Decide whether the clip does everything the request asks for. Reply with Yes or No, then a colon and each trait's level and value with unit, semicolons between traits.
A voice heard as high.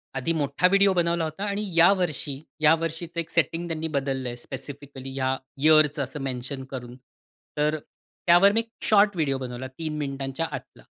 No: medium, 150 Hz